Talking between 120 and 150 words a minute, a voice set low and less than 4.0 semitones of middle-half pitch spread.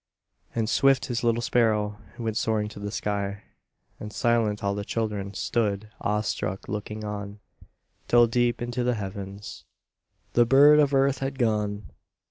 Yes: average, 145 wpm; low, 110 Hz; average, 2.7 semitones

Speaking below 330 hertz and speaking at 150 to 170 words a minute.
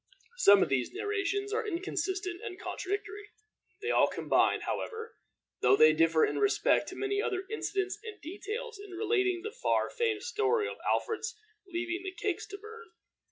No: very high, 405 Hz; average, 160 wpm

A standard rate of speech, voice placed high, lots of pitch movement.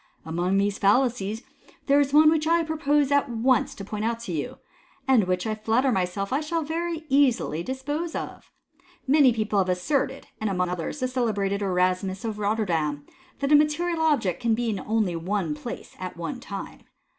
Yes: average, 185 wpm; high, 225 Hz; wide, 6.7 semitones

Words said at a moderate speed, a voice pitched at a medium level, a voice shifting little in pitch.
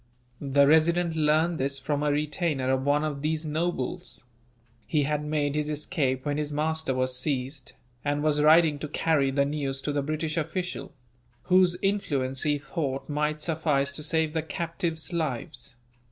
Yes: average, 165 wpm; medium, 150 Hz; narrow, 2.3 semitones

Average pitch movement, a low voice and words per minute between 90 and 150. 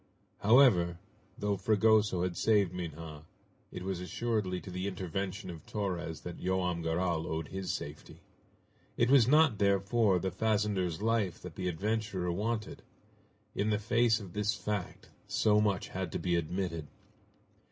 Yes: average, 3.3 semitones; very low, 95 Hz; average, 145 wpm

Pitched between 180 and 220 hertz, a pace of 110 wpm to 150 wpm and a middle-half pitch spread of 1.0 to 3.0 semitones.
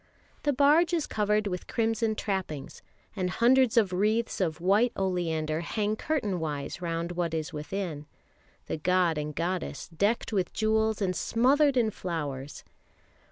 No: high, 190 Hz; average, 145 wpm; average, 5.1 semitones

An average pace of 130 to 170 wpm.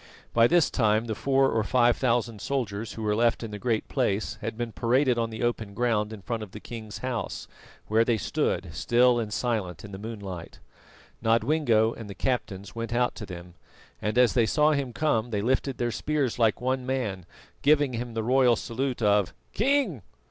No: average, 195 wpm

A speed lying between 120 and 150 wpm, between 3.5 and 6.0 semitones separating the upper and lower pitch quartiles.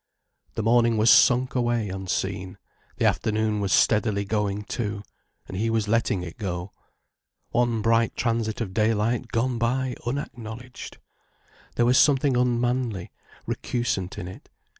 No: slow, 135 wpm; average, 2.8 semitones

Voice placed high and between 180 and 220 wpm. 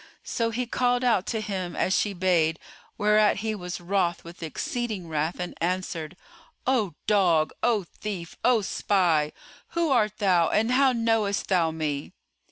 No: high, 195 Hz; average, 155 wpm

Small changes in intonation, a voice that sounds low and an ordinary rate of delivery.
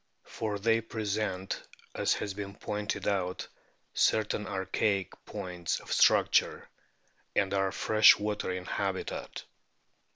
No: narrow, 1.8 semitones; low, 100 Hz; slow, 110 wpm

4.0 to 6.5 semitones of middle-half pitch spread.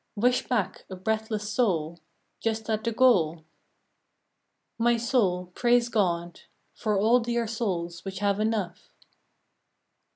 Yes: average, 4.3 semitones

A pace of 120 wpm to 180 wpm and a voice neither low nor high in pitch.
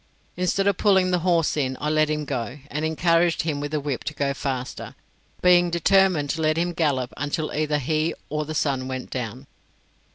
No: average, 195 wpm; medium, 155 Hz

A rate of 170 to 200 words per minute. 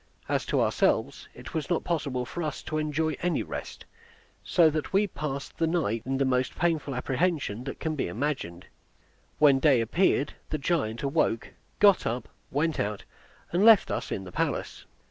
Yes: average, 175 wpm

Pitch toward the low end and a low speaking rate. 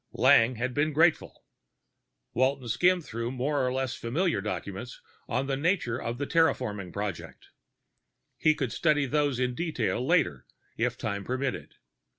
No: low, 130 Hz; average, 145 wpm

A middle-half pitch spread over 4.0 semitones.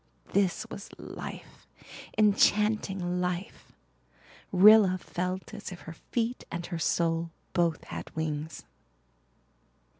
No: average, 3.2 semitones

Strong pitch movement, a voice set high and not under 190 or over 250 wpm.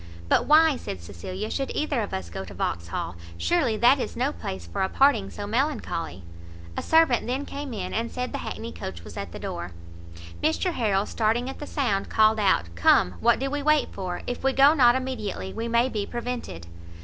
Yes: wide, 6.2 semitones; high, 230 Hz; fast, 205 wpm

